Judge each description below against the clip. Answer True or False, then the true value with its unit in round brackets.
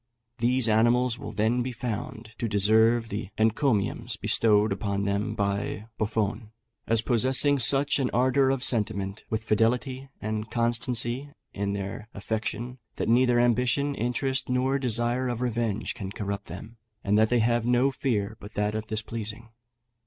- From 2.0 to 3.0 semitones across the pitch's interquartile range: True (2.7 semitones)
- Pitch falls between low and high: False (115 Hz)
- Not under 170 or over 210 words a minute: False (150 wpm)